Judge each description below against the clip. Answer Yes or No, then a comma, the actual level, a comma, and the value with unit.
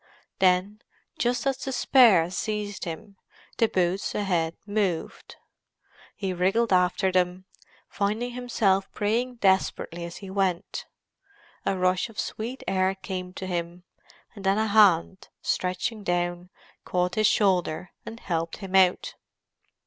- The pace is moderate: No, slow, 125 wpm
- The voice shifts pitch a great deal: No, average, 2.8 semitones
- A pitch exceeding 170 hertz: Yes, high, 190 Hz